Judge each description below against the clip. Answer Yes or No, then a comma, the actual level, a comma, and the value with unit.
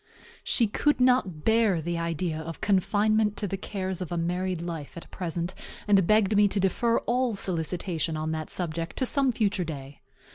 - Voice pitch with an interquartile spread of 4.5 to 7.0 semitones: No, average, 4.0 semitones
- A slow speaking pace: No, average, 180 wpm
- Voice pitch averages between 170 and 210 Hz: Yes, medium, 185 Hz